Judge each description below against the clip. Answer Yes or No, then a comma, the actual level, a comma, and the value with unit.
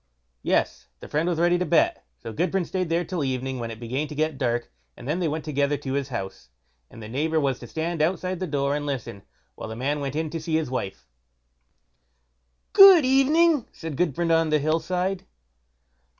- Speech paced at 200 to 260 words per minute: Yes, fast, 205 wpm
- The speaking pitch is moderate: Yes, medium, 155 Hz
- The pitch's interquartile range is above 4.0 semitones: Yes, average, 4.6 semitones